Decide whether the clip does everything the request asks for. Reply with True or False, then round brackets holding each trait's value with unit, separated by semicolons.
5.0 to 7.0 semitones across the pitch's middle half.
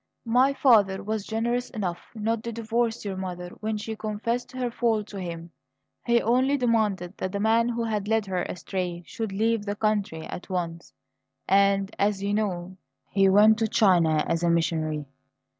False (3.5 semitones)